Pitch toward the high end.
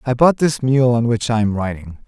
No: low, 120 Hz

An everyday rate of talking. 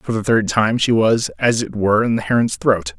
No: fast, 260 wpm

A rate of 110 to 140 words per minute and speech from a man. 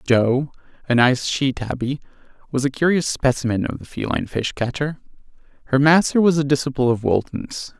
No: average, 160 wpm; male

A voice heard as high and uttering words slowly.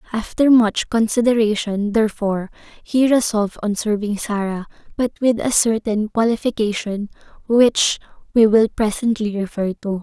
Yes: high, 220 Hz; slow, 120 wpm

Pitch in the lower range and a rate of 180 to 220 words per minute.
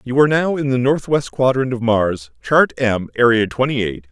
Yes: low, 125 Hz; fast, 205 wpm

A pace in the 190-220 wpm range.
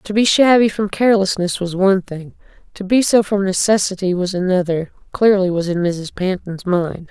No: average, 170 wpm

